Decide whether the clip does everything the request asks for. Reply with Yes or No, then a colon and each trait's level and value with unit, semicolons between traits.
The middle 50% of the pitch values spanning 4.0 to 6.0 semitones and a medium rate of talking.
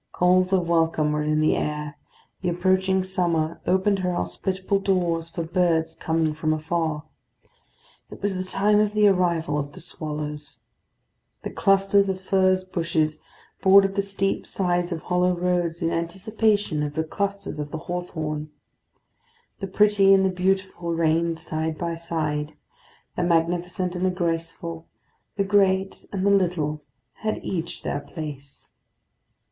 No: average, 3.0 semitones; average, 145 wpm